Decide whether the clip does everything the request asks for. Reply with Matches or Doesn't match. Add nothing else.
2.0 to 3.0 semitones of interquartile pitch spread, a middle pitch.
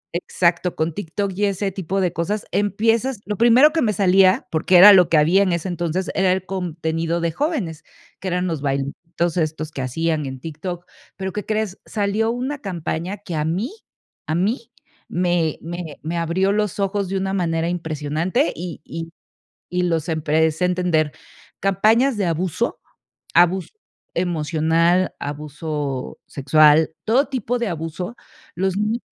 Doesn't match